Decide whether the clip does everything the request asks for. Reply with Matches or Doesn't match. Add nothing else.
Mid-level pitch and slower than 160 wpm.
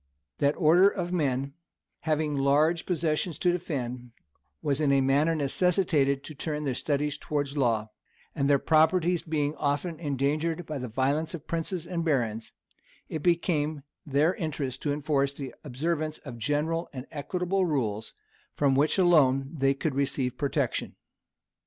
Matches